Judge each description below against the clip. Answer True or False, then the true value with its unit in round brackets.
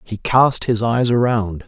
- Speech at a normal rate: True (180 wpm)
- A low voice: True (115 Hz)